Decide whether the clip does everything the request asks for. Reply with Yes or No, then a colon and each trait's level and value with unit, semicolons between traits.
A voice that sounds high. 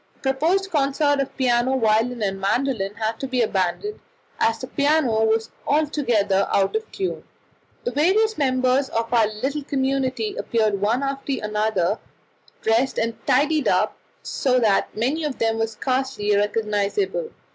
Yes: very high, 255 Hz